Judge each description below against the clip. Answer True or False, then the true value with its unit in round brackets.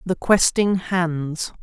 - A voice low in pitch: False (175 Hz)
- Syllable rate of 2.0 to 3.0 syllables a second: True (2.8 syllables/s)